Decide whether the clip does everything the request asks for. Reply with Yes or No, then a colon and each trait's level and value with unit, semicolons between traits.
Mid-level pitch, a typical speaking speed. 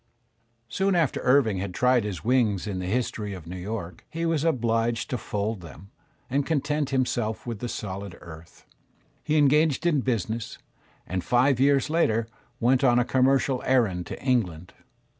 No: low, 120 Hz; average, 165 wpm